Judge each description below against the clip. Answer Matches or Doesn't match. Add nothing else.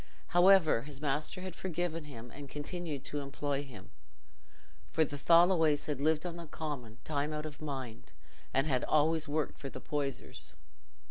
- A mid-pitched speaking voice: Matches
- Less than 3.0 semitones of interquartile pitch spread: Matches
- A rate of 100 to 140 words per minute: Doesn't match